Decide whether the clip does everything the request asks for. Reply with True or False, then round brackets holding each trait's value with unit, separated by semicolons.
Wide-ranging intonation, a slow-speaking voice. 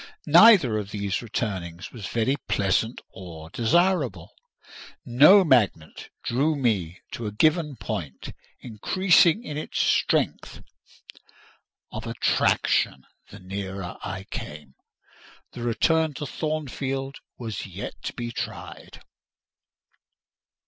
True (7.3 semitones; 105 wpm)